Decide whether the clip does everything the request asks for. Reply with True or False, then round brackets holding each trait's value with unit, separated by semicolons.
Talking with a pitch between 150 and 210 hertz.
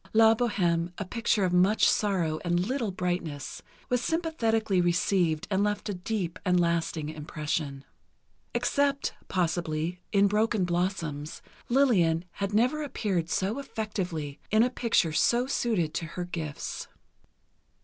True (185 Hz)